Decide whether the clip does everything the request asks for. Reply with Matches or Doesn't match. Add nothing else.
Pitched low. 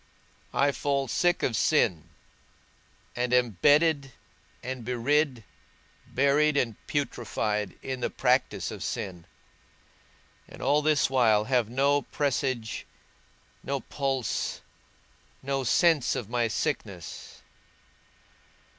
Matches